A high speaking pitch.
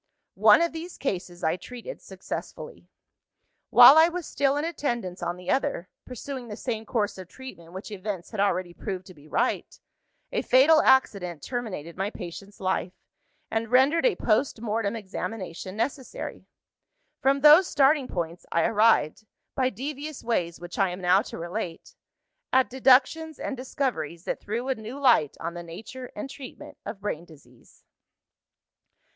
Yes: high, 220 Hz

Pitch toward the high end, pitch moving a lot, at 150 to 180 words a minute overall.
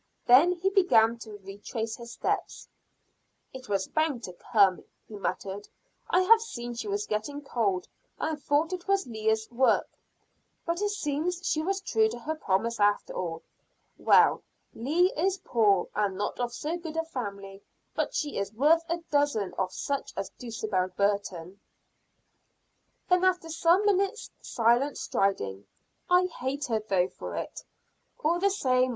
Yes: very high, 250 Hz; wide, 8.4 semitones; average, 155 wpm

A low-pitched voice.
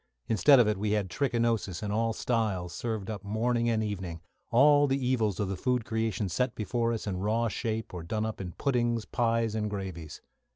Yes: low, 110 Hz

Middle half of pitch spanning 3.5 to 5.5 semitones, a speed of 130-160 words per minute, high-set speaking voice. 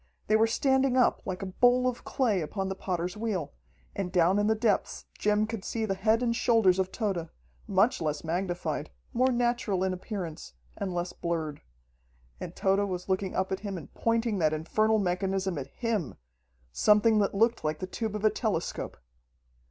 No: average, 3.8 semitones; average, 185 wpm; high, 195 Hz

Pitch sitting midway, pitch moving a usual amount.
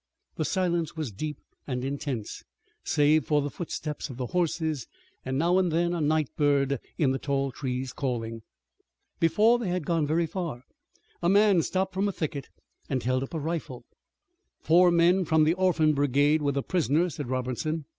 Yes: medium, 155 Hz; average, 4.0 semitones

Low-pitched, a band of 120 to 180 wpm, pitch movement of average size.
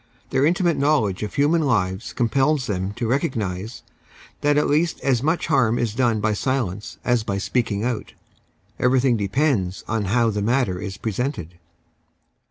Yes: low, 120 Hz; average, 155 wpm; average, 4.9 semitones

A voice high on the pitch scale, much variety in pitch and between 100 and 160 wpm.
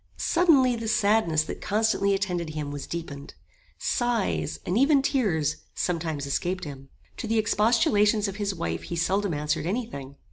Yes: high, 195 Hz; wide, 6.3 semitones; average, 155 wpm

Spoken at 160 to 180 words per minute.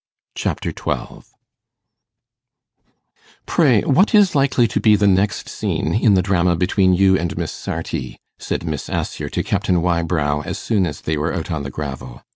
Yes: average, 165 wpm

